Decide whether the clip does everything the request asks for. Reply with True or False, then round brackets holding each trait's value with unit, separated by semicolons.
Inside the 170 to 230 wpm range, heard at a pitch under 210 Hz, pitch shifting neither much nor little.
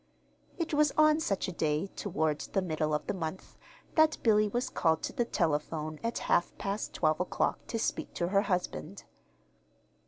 False (175 wpm; 185 Hz; 6.5 semitones)